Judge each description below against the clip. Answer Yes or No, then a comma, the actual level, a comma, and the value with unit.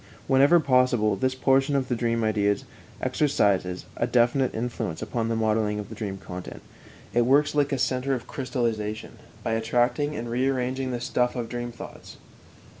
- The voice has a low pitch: Yes, low, 120 Hz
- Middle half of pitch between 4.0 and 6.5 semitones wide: No, average, 2.8 semitones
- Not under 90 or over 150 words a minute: No, average, 170 wpm